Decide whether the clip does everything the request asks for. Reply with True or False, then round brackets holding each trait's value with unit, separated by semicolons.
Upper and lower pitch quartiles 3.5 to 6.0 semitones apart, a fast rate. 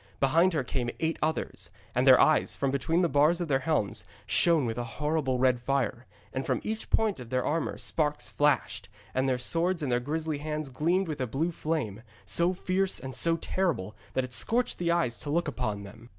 True (4.7 semitones; 210 wpm)